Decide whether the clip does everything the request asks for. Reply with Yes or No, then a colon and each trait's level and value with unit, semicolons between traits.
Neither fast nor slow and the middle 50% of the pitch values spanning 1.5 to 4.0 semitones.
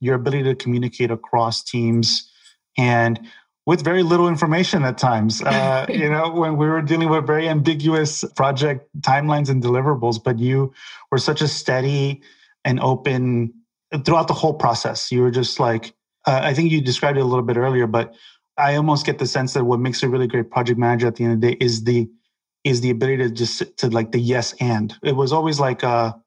Yes: average, 195 wpm; average, 3.7 semitones